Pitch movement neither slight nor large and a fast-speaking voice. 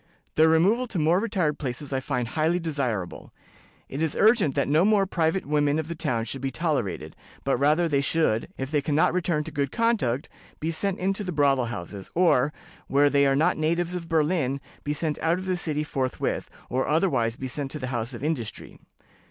Yes: average, 3.9 semitones; fast, 210 wpm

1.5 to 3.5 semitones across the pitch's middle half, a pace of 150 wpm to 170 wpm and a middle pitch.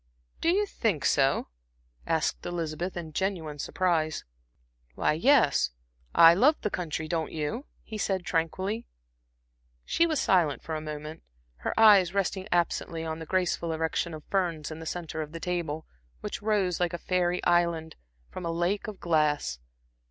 Yes: average, 3.0 semitones; average, 160 wpm; medium, 170 Hz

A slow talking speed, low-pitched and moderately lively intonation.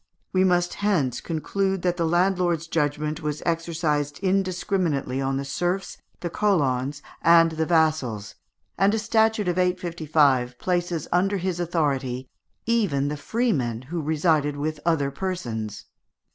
No: slow, 130 wpm; medium, 165 Hz; average, 4.2 semitones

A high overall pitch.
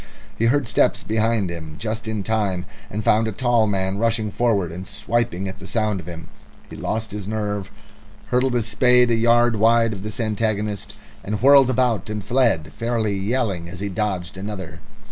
No: low, 110 Hz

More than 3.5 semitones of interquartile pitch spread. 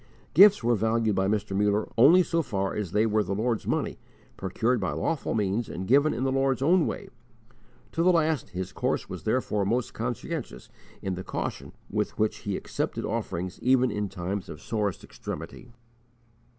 Yes: average, 5.1 semitones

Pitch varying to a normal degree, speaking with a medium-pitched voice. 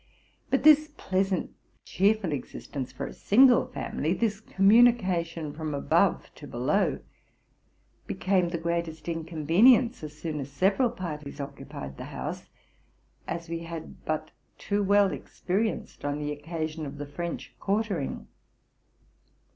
Yes: average, 5.0 semitones; medium, 170 Hz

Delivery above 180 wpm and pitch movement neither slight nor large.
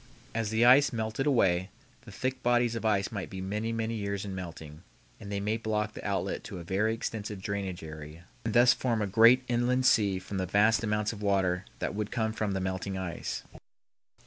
Yes: fast, 205 wpm; average, 3.2 semitones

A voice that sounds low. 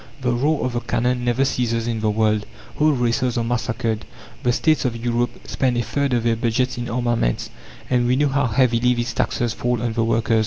Yes: low, 120 Hz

